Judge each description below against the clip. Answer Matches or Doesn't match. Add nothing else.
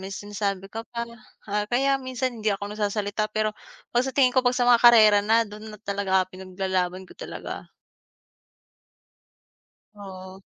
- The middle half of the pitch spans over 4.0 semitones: Doesn't match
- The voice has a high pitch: Matches